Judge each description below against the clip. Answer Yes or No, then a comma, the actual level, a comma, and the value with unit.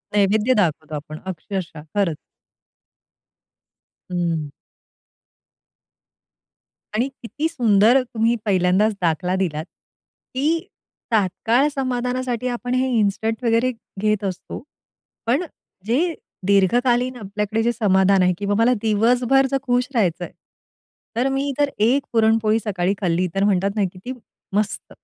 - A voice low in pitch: No, high, 220 Hz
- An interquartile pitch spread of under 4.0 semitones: No, average, 4.5 semitones